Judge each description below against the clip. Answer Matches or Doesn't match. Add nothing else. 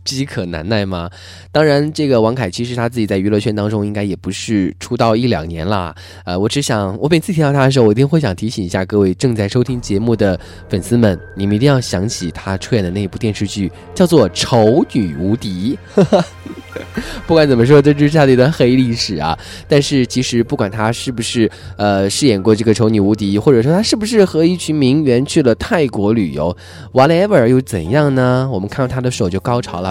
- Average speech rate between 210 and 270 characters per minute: Doesn't match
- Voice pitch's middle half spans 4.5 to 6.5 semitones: Matches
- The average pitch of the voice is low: Matches